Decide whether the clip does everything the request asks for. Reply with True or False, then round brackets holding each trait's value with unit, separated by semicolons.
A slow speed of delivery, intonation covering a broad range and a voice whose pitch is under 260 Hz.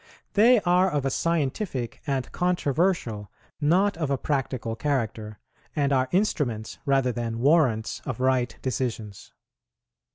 True (125 wpm; 5.8 semitones; 135 Hz)